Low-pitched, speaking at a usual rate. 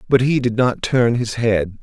No: low, 120 Hz; fast, 230 wpm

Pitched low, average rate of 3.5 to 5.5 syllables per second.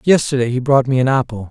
No: low, 130 Hz; 6.4 syllables/s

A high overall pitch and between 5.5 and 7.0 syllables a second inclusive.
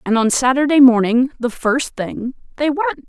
No: very high, 260 Hz; 4.5 syllables/s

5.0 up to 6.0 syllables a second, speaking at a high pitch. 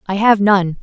No: 4.5 syllables/s; high, 200 Hz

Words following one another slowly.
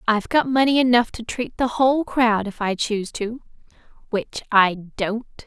No: average, 175 wpm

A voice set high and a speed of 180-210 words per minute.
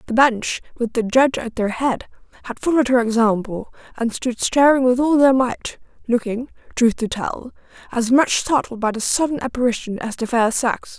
Yes: high, 245 Hz; average, 185 wpm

